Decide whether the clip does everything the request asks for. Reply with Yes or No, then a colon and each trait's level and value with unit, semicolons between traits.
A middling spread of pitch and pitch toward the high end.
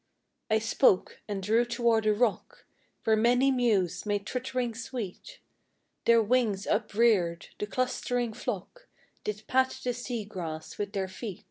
Yes: average, 3.3 semitones; high, 220 Hz